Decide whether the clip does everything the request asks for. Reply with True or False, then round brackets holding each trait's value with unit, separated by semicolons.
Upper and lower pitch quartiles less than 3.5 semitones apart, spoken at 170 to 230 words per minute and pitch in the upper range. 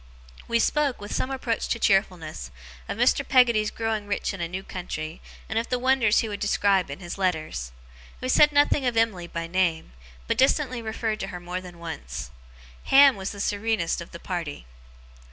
False (5.2 semitones; 190 wpm; 200 Hz)